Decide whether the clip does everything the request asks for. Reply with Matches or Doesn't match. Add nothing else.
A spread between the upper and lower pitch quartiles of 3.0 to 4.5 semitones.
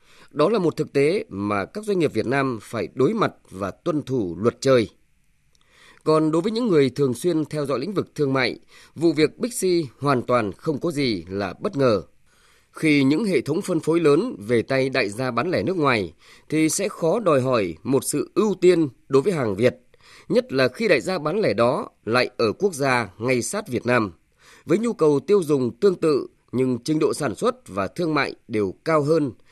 Doesn't match